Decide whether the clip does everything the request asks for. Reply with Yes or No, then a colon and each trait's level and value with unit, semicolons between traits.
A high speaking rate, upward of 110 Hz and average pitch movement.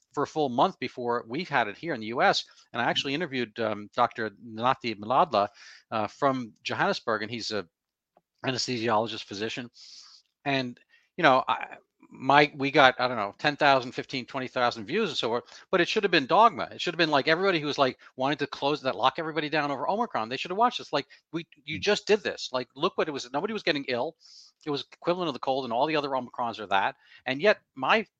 Yes: fast, 225 wpm; low, 135 Hz; average, 4.1 semitones